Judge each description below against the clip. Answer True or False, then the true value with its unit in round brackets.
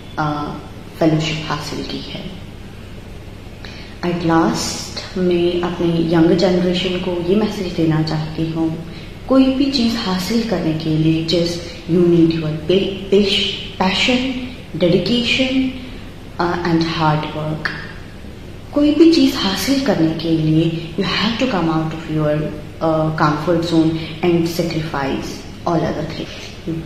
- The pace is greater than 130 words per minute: False (120 wpm)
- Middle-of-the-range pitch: True (165 Hz)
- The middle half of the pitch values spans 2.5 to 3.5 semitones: True (3.1 semitones)